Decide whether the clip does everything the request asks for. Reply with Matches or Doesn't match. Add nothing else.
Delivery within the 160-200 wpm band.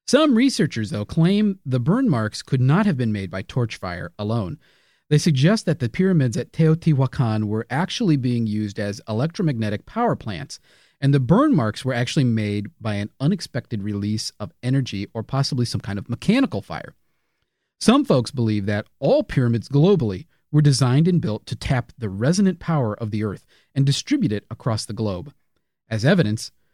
Matches